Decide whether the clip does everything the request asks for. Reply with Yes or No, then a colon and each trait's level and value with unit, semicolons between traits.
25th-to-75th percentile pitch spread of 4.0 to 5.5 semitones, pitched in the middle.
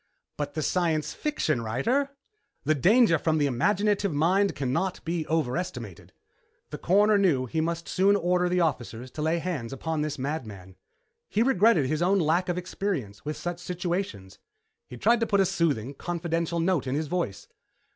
Yes: average, 4.7 semitones; medium, 165 Hz